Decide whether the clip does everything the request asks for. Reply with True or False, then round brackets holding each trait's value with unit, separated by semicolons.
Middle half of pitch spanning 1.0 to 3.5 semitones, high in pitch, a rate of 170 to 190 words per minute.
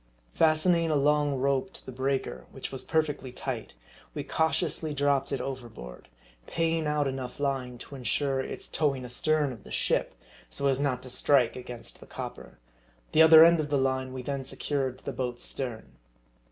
False (2.6 semitones; 135 Hz; 180 wpm)